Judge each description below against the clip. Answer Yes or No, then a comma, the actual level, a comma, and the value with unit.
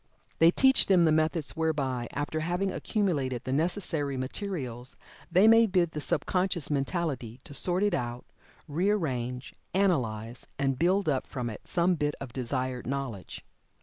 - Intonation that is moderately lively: No, wide, 5.7 semitones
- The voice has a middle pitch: Yes, medium, 150 Hz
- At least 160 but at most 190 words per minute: No, average, 150 wpm